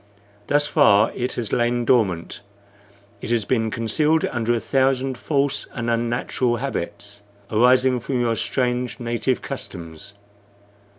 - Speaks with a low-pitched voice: Yes, low, 120 Hz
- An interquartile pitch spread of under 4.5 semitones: Yes, narrow, 2.6 semitones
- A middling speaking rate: No, slow, 125 wpm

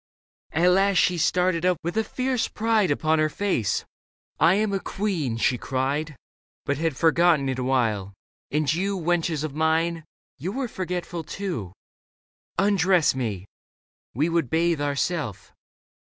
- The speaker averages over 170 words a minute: No, average, 150 wpm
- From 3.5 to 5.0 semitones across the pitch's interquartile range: Yes, average, 4.4 semitones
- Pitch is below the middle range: No, medium, 165 Hz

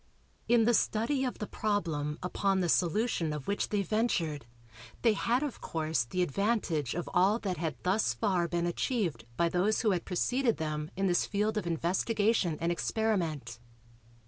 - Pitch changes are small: No, average, 4.8 semitones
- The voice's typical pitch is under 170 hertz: No, medium, 185 Hz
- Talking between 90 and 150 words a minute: No, average, 170 wpm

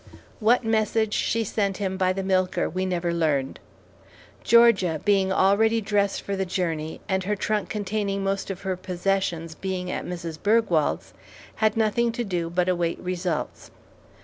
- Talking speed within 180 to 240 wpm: No, average, 155 wpm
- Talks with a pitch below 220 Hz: Yes, high, 190 Hz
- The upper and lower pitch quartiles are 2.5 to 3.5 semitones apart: Yes, average, 2.8 semitones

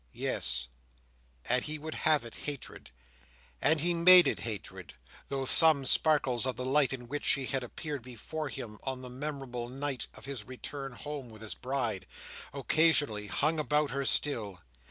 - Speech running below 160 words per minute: No, average, 165 wpm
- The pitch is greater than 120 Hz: Yes, low, 135 Hz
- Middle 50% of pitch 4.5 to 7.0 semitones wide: No, average, 3.6 semitones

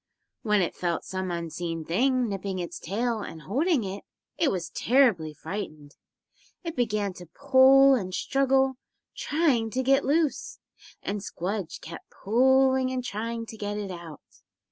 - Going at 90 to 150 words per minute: Yes, average, 145 wpm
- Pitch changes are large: Yes, wide, 6.3 semitones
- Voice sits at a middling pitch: No, high, 215 Hz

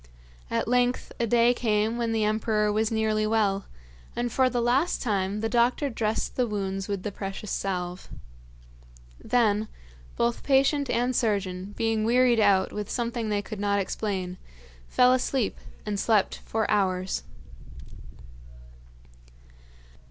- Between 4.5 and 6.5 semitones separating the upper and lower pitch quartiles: No, average, 2.9 semitones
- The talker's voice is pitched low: No, high, 215 Hz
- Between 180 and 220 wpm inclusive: No, slow, 135 wpm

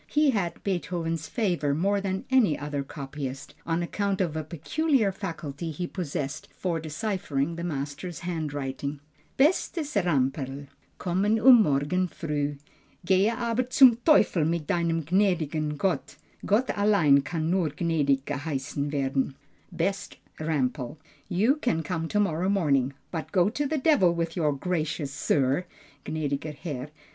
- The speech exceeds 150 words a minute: No, slow, 135 wpm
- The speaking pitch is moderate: Yes, medium, 165 Hz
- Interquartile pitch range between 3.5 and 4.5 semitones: No, average, 5.1 semitones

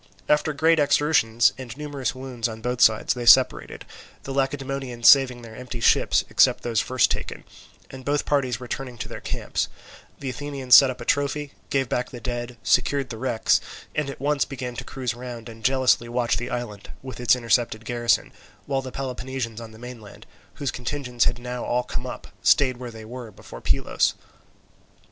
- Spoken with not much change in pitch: Yes, narrow, 2.2 semitones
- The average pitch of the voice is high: No, low, 125 Hz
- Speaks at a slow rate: No, average, 180 wpm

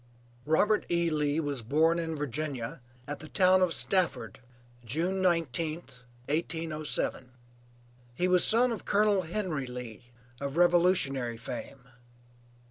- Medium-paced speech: No, slow, 120 wpm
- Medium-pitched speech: Yes, medium, 160 Hz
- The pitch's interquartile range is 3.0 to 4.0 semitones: No, average, 4.5 semitones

